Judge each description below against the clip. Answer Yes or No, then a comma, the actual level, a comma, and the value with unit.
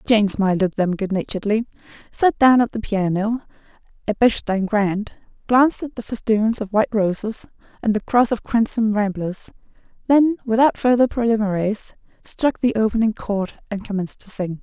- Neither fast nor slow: Yes, average, 160 wpm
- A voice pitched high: Yes, high, 215 Hz